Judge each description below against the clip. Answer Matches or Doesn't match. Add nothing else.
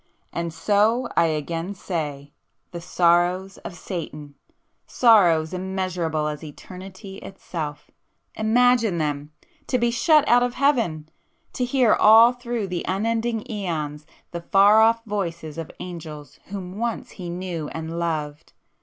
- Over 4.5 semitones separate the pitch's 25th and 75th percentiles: Matches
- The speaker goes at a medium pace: Doesn't match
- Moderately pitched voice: Matches